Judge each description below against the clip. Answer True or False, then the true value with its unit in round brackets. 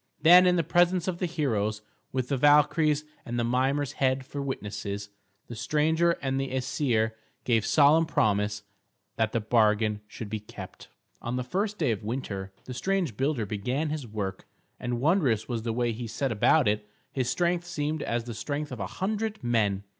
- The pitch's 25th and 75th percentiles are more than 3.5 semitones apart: True (5.6 semitones)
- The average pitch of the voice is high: False (125 Hz)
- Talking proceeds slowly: False (180 wpm)